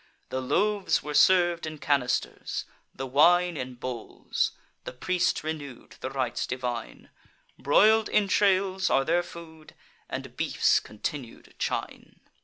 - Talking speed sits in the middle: No, slow, 120 wpm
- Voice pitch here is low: No, medium, 155 Hz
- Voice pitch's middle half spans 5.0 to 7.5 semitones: Yes, wide, 5.6 semitones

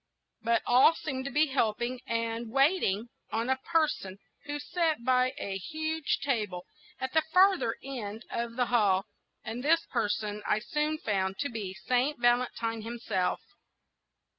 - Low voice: No, high, 240 Hz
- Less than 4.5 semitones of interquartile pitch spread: No, average, 4.8 semitones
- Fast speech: No, average, 145 wpm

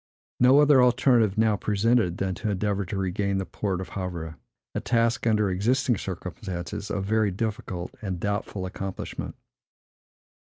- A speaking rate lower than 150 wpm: Yes, average, 140 wpm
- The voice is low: Yes, low, 100 Hz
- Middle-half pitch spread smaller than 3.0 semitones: No, average, 3.3 semitones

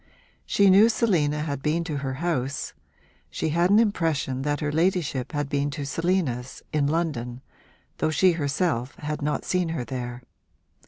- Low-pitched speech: No, medium, 150 Hz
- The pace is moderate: Yes, average, 160 wpm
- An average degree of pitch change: Yes, average, 3.9 semitones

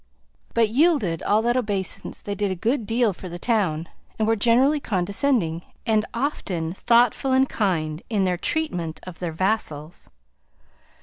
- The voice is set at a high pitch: Yes, high, 205 Hz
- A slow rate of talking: No, average, 150 wpm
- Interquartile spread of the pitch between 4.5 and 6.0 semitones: Yes, wide, 5.4 semitones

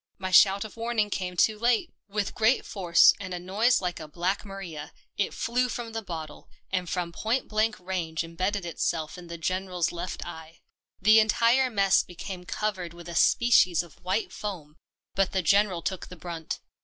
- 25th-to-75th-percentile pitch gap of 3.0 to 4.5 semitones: Yes, average, 3.7 semitones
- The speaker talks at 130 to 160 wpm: No, average, 180 wpm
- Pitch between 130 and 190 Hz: Yes, medium, 185 Hz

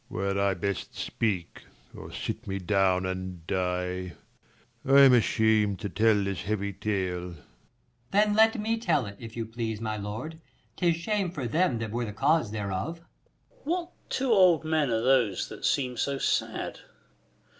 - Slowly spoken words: No, average, 175 wpm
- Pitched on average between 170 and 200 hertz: No, low, 110 Hz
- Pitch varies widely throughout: Yes, wide, 8.1 semitones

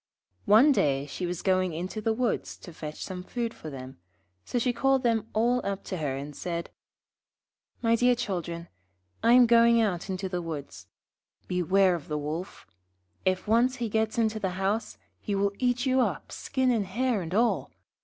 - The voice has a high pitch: Yes, high, 200 Hz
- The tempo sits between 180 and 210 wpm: Yes, average, 185 wpm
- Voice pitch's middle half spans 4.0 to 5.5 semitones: Yes, average, 5.0 semitones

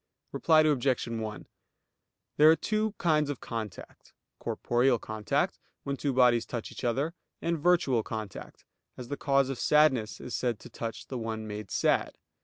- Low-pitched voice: Yes, low, 125 Hz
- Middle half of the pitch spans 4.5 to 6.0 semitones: Yes, average, 4.9 semitones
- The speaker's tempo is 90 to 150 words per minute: No, average, 160 wpm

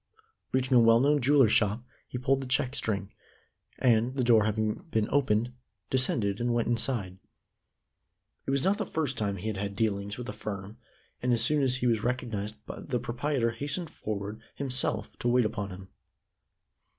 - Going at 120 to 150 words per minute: No, average, 175 wpm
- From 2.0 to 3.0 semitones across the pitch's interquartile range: No, average, 3.5 semitones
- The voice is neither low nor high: No, low, 120 Hz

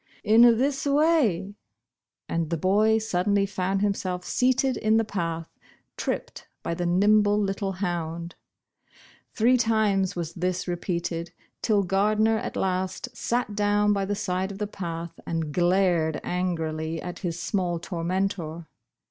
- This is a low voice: No, high, 190 Hz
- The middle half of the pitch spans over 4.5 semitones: No, average, 3.3 semitones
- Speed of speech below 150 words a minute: Yes, average, 140 wpm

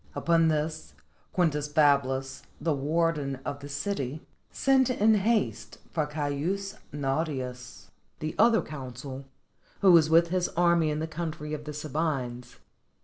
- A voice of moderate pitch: Yes, medium, 155 Hz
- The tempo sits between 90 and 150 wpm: Yes, slow, 135 wpm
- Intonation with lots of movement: No, average, 3.3 semitones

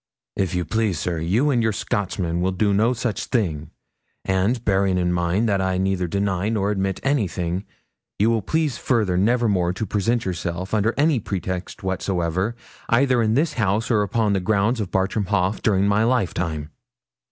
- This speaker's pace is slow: No, average, 175 wpm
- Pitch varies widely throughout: No, average, 3.5 semitones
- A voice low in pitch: Yes, low, 100 Hz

